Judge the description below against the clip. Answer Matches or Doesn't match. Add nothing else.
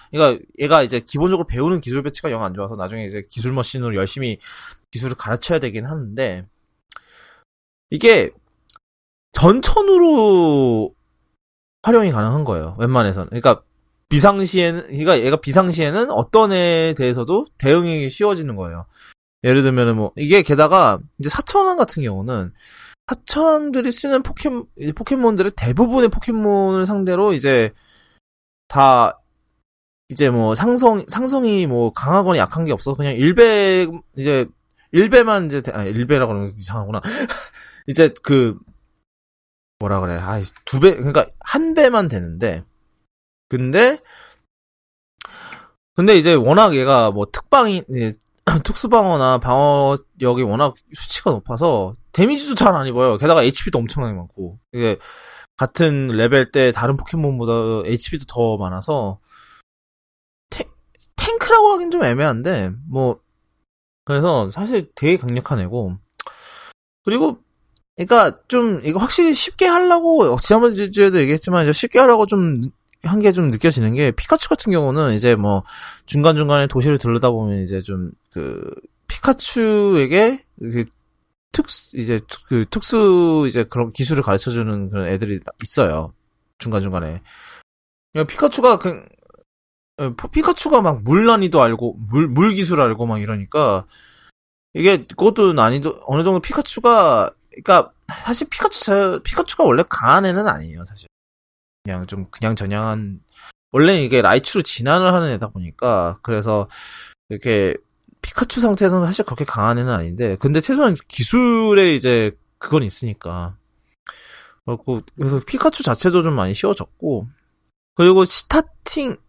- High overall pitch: Doesn't match